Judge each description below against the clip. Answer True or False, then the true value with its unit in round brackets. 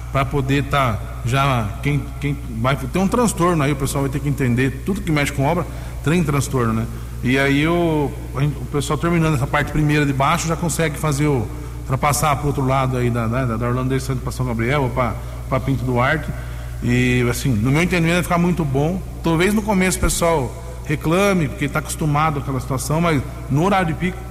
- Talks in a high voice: False (140 Hz)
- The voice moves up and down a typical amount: True (3.7 semitones)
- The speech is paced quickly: True (210 wpm)